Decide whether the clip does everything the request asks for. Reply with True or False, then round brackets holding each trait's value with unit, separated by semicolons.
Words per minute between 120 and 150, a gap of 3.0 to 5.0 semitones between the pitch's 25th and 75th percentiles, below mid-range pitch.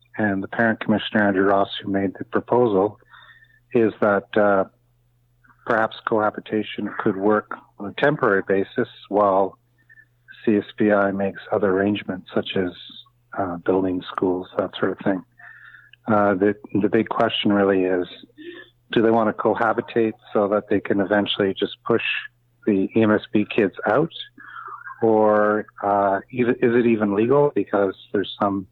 False (140 wpm; 2.5 semitones; 105 Hz)